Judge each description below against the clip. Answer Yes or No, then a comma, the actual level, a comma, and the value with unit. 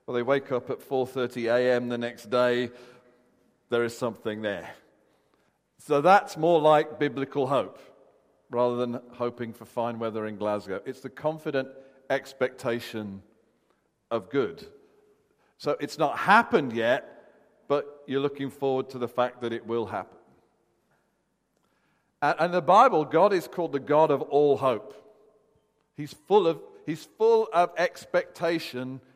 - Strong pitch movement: No, average, 4.3 semitones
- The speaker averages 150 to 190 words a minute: No, average, 140 wpm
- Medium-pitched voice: No, low, 130 Hz